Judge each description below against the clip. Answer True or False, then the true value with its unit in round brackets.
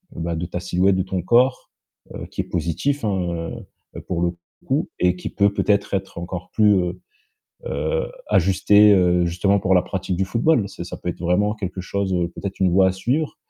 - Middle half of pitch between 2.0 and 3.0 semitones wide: True (2.4 semitones)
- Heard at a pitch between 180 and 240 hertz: False (95 Hz)